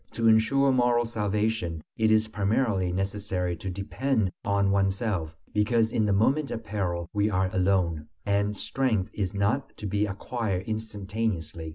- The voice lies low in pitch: Yes, low, 105 Hz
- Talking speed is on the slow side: No, average, 150 wpm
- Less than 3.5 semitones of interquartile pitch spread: Yes, average, 2.8 semitones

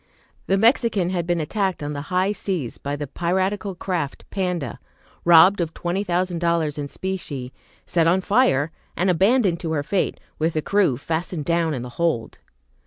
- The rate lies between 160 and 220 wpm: Yes, average, 175 wpm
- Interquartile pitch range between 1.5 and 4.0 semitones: Yes, average, 3.5 semitones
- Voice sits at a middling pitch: Yes, medium, 170 Hz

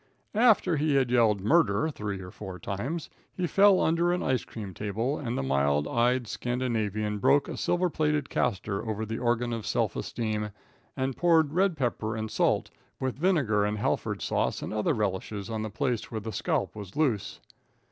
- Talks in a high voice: No, low, 115 Hz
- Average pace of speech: Yes, average, 180 wpm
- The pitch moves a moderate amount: No, wide, 5.7 semitones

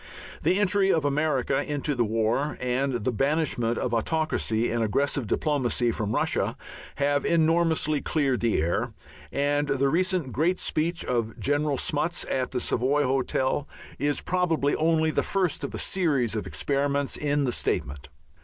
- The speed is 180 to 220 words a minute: No, average, 150 wpm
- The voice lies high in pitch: No, medium, 140 Hz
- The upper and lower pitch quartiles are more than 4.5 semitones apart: No, average, 4.1 semitones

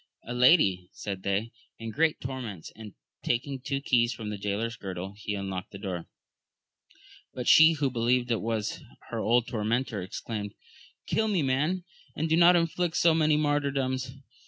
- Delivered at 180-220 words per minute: No, average, 165 wpm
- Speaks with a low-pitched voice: Yes, low, 120 Hz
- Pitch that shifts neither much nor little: No, wide, 5.8 semitones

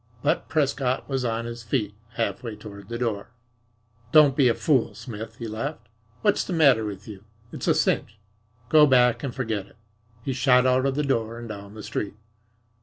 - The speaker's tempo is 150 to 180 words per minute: No, average, 190 wpm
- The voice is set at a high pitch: No, low, 120 Hz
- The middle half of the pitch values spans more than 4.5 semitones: No, average, 3.7 semitones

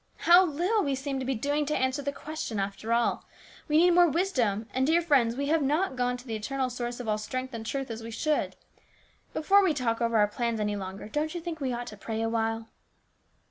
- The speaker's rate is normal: No, fast, 230 wpm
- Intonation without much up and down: No, average, 5.1 semitones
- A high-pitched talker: Yes, very high, 255 Hz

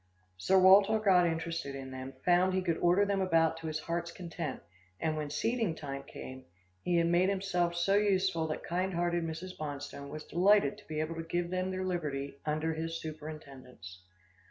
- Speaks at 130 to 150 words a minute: No, average, 185 wpm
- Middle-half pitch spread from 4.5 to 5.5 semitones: No, average, 3.2 semitones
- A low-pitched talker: No, medium, 165 Hz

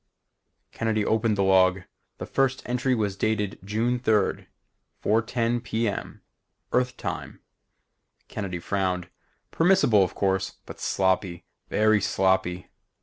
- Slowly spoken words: Yes, slow, 115 wpm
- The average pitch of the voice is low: Yes, low, 105 Hz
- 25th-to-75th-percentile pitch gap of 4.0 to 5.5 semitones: No, average, 3.4 semitones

